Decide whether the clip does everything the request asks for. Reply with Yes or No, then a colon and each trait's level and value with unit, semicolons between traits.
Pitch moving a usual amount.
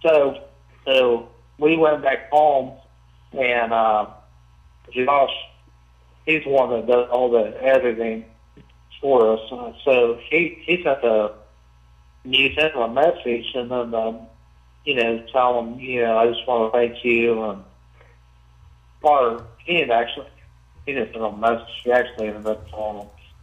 No: wide, 8.2 semitones